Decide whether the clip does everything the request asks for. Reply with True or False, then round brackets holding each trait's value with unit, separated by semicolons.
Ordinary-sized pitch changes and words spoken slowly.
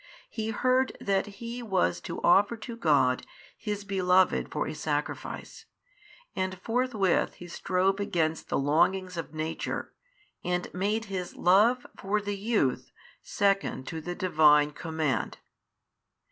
True (4.3 semitones; 130 wpm)